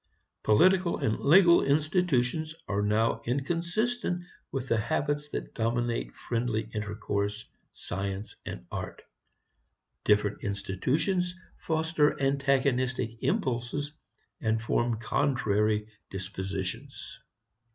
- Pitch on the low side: Yes, low, 125 Hz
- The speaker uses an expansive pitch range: Yes, wide, 6.4 semitones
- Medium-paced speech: No, slow, 90 wpm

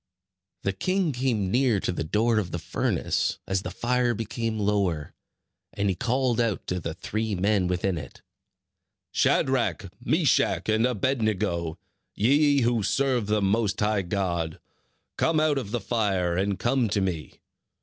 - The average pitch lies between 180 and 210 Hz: No, low, 105 Hz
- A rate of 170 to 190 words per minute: No, average, 155 wpm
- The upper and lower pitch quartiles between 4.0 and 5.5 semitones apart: Yes, average, 4.3 semitones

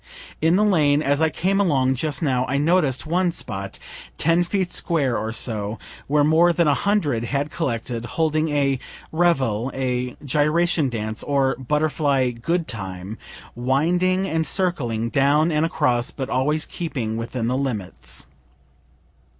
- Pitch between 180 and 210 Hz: No, medium, 145 Hz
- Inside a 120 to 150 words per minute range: Yes, average, 145 wpm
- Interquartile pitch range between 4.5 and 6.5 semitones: Yes, average, 4.8 semitones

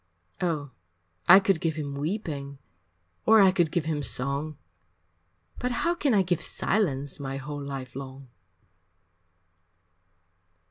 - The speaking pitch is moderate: Yes, medium, 150 Hz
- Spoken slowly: Yes, slow, 125 wpm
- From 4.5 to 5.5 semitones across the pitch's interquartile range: Yes, average, 5.1 semitones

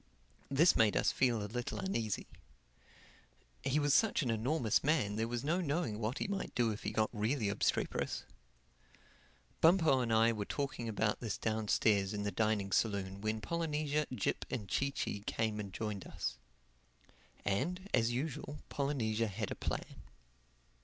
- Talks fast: No, average, 160 wpm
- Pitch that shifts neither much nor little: Yes, average, 5.0 semitones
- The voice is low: Yes, low, 115 Hz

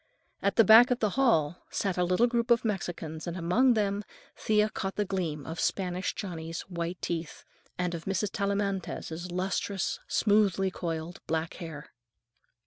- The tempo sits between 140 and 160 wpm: Yes, average, 155 wpm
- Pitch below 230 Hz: Yes, medium, 185 Hz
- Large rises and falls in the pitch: No, average, 3.6 semitones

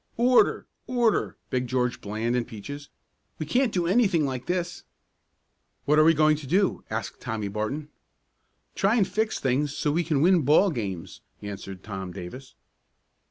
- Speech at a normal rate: Yes, average, 160 wpm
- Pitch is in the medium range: Yes, medium, 145 Hz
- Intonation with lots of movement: Yes, wide, 7.4 semitones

